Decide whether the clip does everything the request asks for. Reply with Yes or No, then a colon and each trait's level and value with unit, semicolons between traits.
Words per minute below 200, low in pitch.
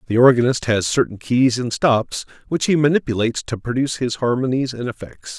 Yes: average, 180 wpm; low, 125 Hz